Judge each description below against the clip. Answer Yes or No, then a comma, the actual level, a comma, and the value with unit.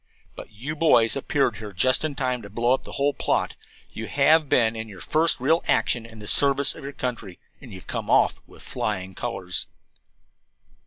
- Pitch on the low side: Yes, low, 125 Hz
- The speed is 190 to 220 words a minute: Yes, average, 200 wpm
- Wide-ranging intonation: No, average, 4.5 semitones